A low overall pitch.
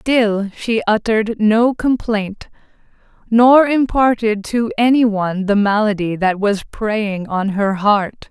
No: high, 215 Hz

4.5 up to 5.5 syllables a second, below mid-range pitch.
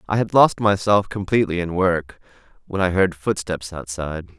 Yes: 5.1 syllables/s; very low, 90 Hz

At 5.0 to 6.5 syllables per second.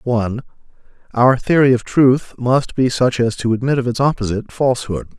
Yes: 5.7 syllables/s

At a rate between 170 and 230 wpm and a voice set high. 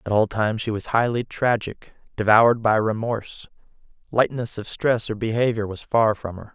No: average, 175 wpm; low, 110 Hz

